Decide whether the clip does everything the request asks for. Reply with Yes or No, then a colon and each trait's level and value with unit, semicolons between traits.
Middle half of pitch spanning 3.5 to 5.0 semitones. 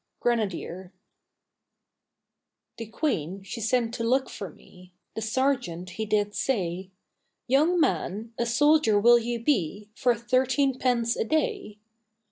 Yes: average, 4.5 semitones